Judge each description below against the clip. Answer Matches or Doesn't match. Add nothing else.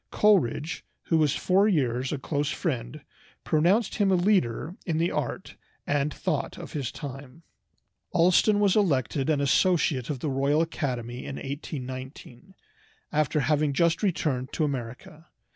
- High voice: Doesn't match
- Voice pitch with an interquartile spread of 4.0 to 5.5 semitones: Matches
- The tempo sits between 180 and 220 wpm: Doesn't match